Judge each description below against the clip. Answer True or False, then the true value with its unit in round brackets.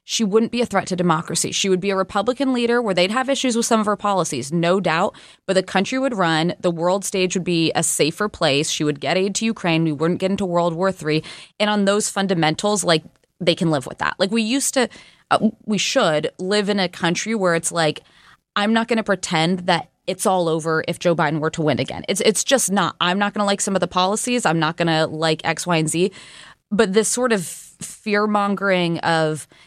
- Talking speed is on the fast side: True (240 wpm)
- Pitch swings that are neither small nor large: True (4.0 semitones)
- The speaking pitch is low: False (185 Hz)